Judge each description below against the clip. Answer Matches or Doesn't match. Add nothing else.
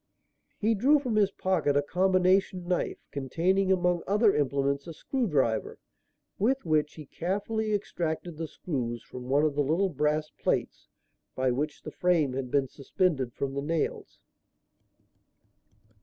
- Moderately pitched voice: Matches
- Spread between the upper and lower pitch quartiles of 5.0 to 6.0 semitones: Matches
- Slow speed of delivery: Doesn't match